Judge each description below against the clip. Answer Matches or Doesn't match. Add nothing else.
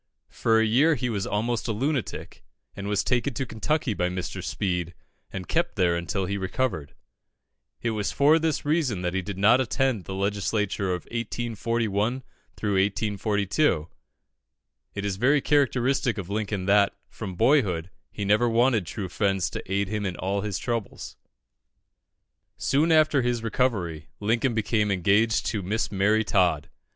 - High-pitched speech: Doesn't match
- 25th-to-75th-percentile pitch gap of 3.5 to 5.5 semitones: Matches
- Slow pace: Doesn't match